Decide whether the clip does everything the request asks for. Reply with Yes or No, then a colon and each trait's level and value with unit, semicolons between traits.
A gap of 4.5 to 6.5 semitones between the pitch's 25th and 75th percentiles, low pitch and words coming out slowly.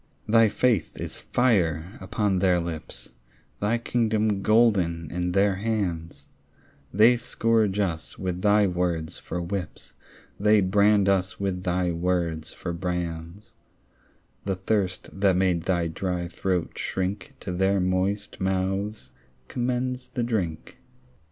No: average, 3.1 semitones; very low, 95 Hz; slow, 125 wpm